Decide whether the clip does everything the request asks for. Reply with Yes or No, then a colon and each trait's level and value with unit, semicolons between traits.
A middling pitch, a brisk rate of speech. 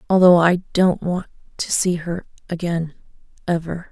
No: medium, 175 Hz; average, 140 wpm